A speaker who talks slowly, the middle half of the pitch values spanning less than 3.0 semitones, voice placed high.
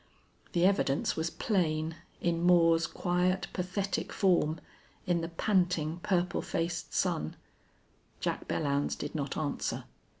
No: slow, 120 wpm; narrow, 2.4 semitones; medium, 170 Hz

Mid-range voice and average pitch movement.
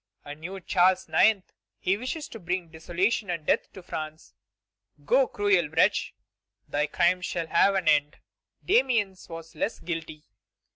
Yes: medium, 180 Hz; average, 3.8 semitones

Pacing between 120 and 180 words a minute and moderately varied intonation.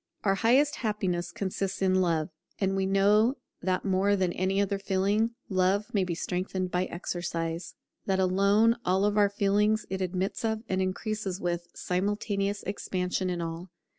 No: average, 155 wpm; narrow, 1.9 semitones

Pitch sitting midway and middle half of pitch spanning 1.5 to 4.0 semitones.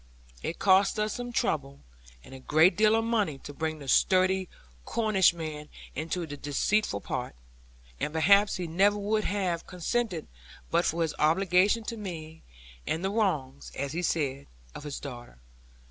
No: medium, 175 Hz; average, 5.1 semitones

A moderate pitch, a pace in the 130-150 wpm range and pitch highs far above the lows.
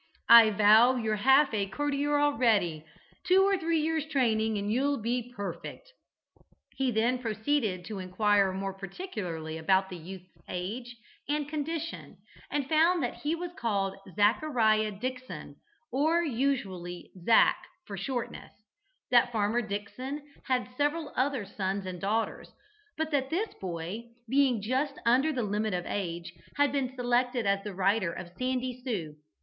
No: high, 235 Hz; average, 145 wpm; wide, 6.0 semitones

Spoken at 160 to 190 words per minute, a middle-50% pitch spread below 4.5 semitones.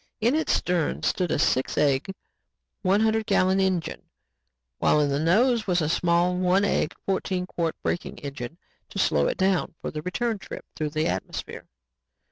Yes: average, 170 wpm; average, 4.0 semitones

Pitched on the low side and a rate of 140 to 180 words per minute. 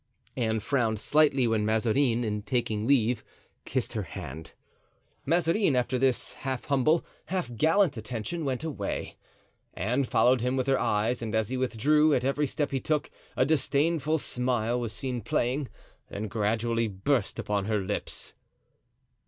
Yes: low, 125 Hz; average, 150 wpm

